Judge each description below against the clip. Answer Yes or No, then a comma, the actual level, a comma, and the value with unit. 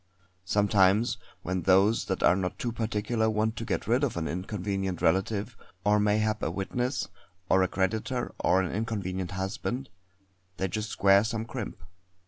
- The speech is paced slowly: No, average, 155 wpm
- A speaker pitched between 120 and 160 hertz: No, low, 105 Hz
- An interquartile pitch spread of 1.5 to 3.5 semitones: Yes, average, 2.8 semitones